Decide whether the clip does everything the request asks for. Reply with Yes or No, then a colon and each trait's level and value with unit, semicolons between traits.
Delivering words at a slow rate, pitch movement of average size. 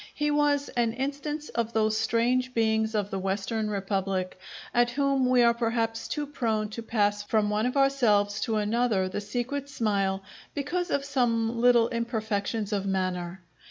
No: average, 160 wpm; average, 3.5 semitones